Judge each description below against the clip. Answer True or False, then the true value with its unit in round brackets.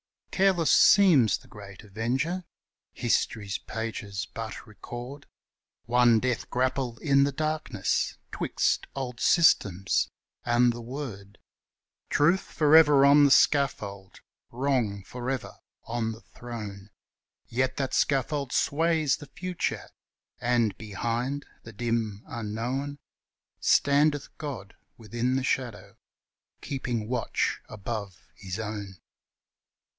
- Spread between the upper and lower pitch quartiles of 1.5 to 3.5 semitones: False (4.5 semitones)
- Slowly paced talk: True (105 wpm)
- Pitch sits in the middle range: False (120 Hz)